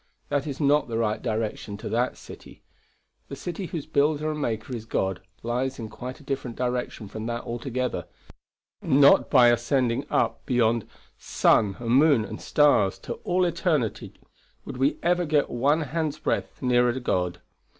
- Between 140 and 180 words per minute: Yes, average, 160 wpm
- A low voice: Yes, low, 125 Hz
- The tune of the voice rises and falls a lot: No, average, 4.1 semitones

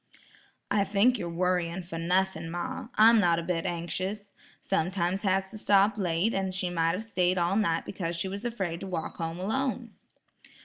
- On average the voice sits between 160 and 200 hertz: Yes, medium, 185 Hz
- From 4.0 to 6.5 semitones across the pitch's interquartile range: No, average, 2.8 semitones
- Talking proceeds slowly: No, average, 180 wpm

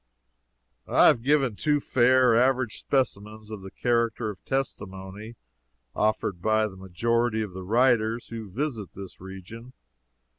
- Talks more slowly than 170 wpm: Yes, average, 140 wpm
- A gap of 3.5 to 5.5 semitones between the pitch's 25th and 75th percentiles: Yes, average, 3.8 semitones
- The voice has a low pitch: Yes, low, 110 Hz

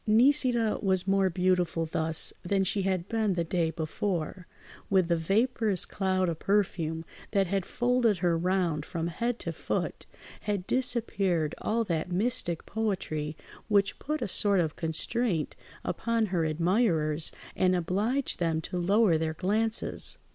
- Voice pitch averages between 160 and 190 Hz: Yes, medium, 185 Hz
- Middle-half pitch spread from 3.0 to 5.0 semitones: Yes, average, 4.4 semitones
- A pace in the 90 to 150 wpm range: Yes, average, 145 wpm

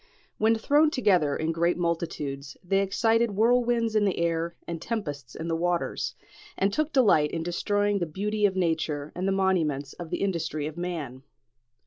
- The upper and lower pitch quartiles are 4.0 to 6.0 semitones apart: Yes, average, 4.3 semitones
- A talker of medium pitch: Yes, medium, 175 Hz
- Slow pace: No, average, 170 wpm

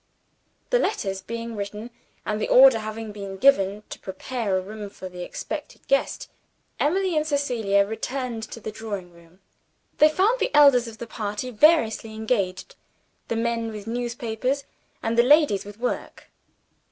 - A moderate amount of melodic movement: Yes, average, 3.8 semitones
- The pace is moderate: Yes, average, 155 wpm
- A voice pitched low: No, high, 225 Hz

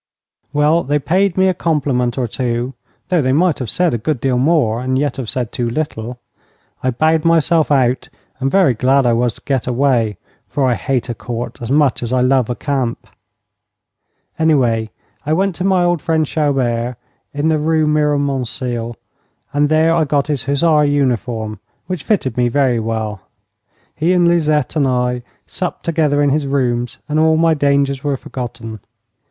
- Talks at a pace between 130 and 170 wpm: No, average, 180 wpm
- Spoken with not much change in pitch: No, average, 4.1 semitones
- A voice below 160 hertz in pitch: Yes, medium, 140 Hz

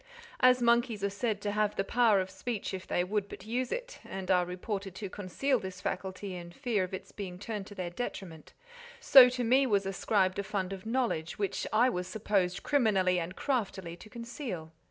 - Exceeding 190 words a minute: Yes, average, 200 wpm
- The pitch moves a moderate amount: Yes, average, 4.1 semitones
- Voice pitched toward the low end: No, high, 200 Hz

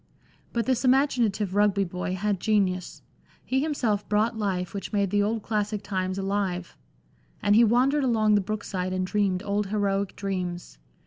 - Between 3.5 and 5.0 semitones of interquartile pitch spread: No, narrow, 2.5 semitones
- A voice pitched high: Yes, high, 205 Hz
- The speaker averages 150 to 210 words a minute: Yes, average, 165 wpm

